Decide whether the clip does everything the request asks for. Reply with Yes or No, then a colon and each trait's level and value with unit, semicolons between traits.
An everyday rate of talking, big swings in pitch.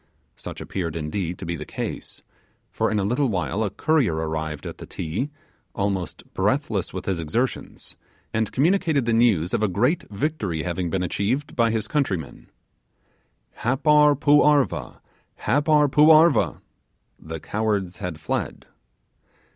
Yes: average, 145 wpm; wide, 8.5 semitones